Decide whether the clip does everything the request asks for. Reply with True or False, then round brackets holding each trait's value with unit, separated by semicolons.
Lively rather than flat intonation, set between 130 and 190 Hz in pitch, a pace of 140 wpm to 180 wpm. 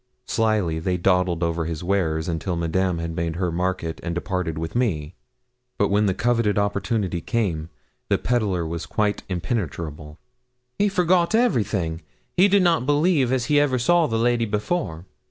False (6.3 semitones; 95 Hz; 160 wpm)